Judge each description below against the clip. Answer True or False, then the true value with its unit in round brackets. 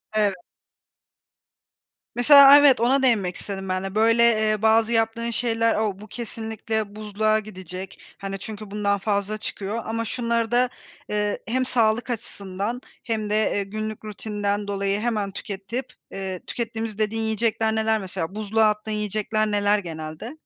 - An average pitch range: False (2.0 semitones)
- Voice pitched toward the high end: True (215 Hz)